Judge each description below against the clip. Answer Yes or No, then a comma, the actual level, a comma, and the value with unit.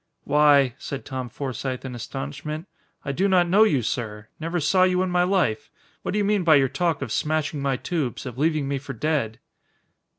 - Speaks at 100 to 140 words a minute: No, average, 200 wpm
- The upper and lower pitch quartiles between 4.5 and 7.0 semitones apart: Yes, average, 4.8 semitones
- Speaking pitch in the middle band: Yes, medium, 145 Hz